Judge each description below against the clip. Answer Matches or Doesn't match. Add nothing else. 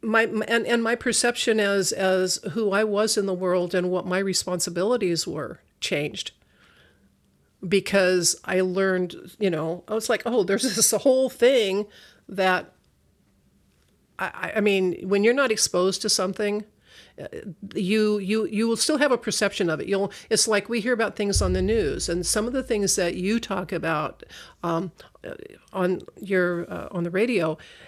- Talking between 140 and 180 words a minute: Matches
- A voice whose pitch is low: Doesn't match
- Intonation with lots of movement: Doesn't match